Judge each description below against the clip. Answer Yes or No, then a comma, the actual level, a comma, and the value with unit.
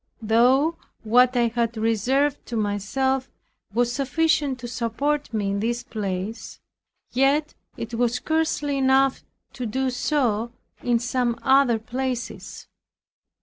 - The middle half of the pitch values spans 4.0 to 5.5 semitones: No, average, 2.9 semitones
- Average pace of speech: No, slow, 120 wpm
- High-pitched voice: Yes, high, 245 Hz